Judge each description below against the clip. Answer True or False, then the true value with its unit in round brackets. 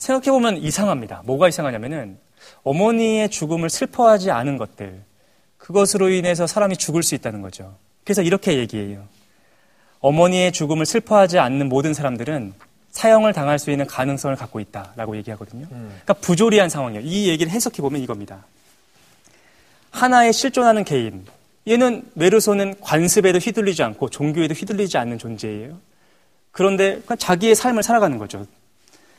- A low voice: False (160 Hz)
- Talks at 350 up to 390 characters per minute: True (380 characters per minute)